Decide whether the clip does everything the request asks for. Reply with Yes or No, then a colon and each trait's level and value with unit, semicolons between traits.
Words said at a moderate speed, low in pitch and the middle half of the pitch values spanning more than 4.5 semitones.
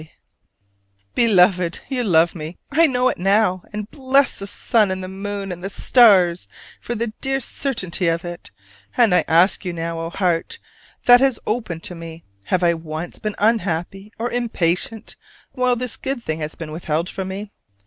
No: average, 180 wpm; high, 190 Hz; wide, 5.4 semitones